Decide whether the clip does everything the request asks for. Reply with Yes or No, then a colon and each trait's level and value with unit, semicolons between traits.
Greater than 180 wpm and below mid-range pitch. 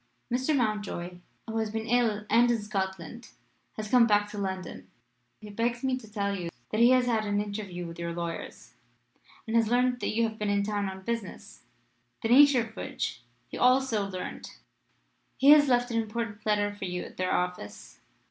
No: average, 195 wpm; high, 215 Hz